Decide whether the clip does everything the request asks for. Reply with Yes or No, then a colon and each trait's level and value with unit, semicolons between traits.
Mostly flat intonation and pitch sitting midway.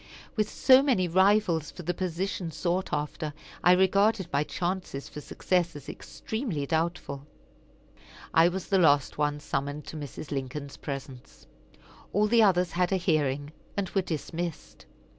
No: average, 4.3 semitones; medium, 170 Hz